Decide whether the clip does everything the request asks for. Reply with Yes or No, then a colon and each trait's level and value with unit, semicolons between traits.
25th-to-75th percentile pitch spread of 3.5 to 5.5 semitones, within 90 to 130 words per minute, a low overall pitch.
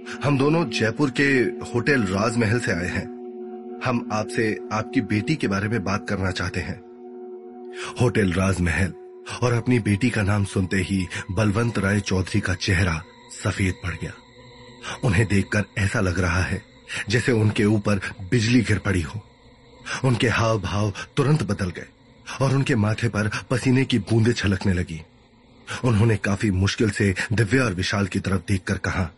No: average, 3.9 semitones; average, 155 wpm; low, 110 Hz